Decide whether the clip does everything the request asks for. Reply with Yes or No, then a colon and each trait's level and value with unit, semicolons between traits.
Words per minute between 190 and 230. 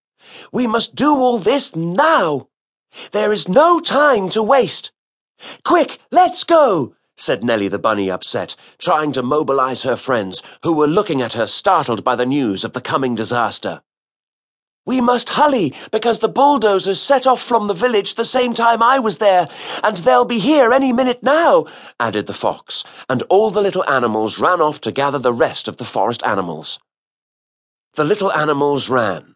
No: average, 170 wpm